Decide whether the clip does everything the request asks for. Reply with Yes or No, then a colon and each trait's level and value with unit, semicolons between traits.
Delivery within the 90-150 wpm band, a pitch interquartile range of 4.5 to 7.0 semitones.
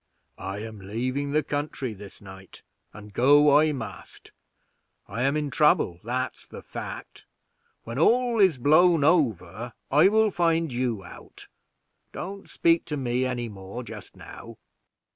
Yes: average, 145 wpm; wide, 5.5 semitones